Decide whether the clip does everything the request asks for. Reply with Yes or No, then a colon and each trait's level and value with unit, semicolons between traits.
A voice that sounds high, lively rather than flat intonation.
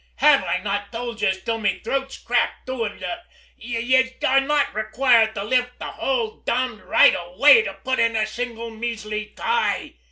No: high, 235 Hz; average, 3.4 semitones